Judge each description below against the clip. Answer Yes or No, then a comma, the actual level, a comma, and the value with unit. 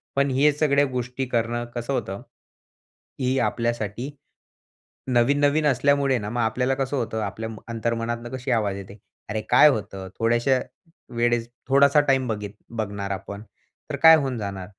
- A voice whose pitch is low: Yes, low, 120 Hz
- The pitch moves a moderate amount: Yes, average, 3.6 semitones